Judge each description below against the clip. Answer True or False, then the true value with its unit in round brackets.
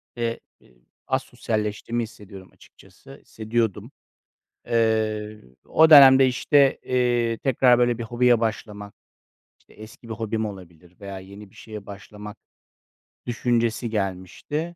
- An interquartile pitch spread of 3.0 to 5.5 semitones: False (2.6 semitones)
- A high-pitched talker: False (110 Hz)